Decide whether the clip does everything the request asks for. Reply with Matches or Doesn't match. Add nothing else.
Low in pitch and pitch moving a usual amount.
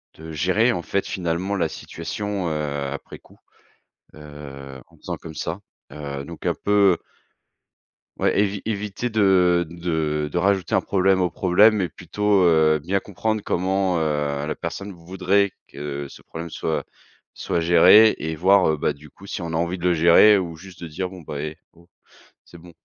Matches